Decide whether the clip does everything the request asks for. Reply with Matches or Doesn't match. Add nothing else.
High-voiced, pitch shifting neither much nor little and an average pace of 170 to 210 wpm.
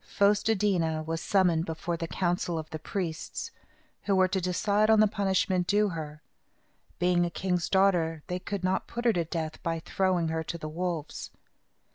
Doesn't match